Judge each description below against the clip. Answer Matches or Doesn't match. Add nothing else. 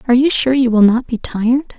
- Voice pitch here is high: Matches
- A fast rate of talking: Matches